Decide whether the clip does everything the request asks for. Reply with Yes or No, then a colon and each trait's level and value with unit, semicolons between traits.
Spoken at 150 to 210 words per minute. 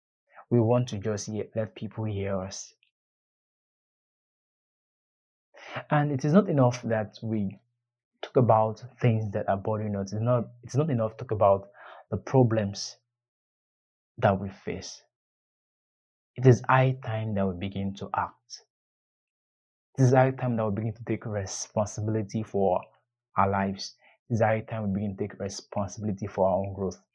Yes: average, 155 wpm